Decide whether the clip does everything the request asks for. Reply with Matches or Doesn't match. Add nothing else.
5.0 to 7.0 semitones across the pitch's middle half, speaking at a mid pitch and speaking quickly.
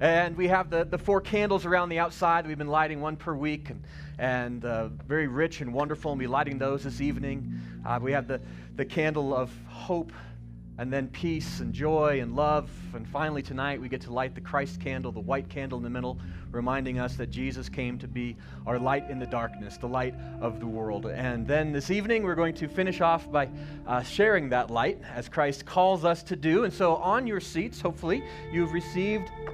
Matches